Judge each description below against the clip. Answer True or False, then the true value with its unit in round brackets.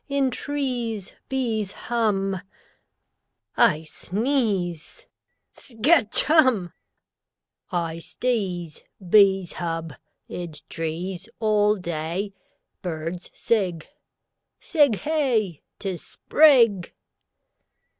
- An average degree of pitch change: False (5.7 semitones)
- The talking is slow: True (75 wpm)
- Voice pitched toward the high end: True (200 Hz)